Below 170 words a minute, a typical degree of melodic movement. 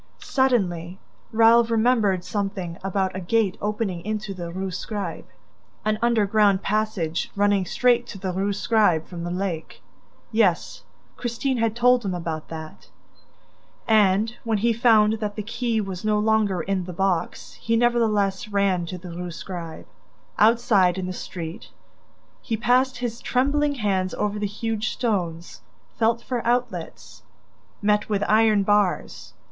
Yes: average, 145 wpm; average, 3.5 semitones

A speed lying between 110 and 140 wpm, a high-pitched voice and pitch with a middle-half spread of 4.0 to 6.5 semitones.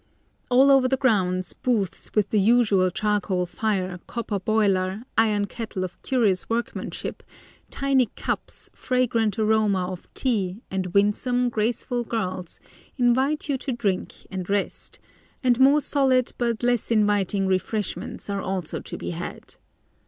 Yes: slow, 135 wpm; high, 215 Hz; average, 4.3 semitones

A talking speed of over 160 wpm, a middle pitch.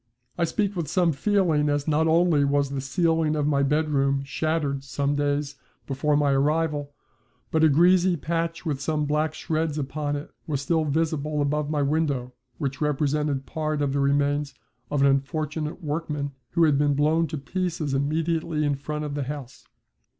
Yes: average, 170 wpm; medium, 150 Hz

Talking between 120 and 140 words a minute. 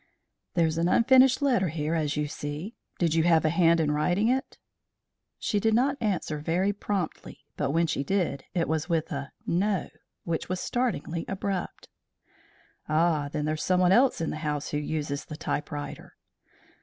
No: average, 170 wpm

